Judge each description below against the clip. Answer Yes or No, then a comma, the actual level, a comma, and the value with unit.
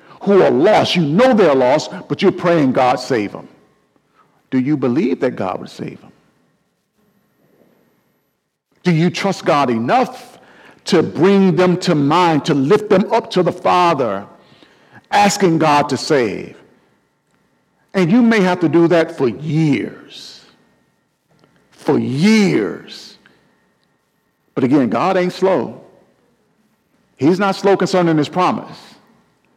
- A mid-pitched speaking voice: Yes, medium, 180 Hz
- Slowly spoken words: Yes, slow, 130 wpm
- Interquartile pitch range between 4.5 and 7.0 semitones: No, average, 3.6 semitones